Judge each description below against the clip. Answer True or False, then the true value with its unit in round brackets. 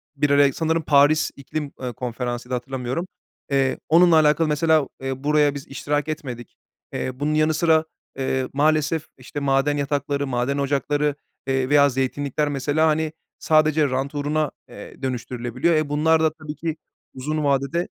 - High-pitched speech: False (145 Hz)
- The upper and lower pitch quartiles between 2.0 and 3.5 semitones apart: True (2.5 semitones)